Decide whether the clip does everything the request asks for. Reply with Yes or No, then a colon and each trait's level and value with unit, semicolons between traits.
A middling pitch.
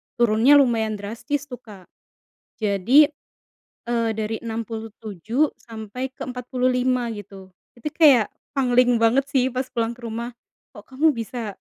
No: high, 235 Hz